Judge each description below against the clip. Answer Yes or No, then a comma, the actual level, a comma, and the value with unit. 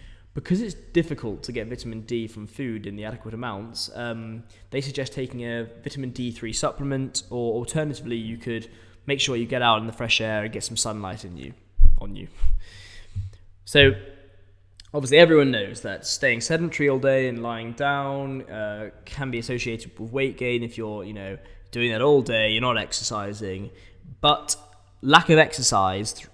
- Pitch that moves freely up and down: No, average, 4.7 semitones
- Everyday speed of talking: Yes, average, 180 wpm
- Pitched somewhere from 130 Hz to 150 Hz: No, low, 115 Hz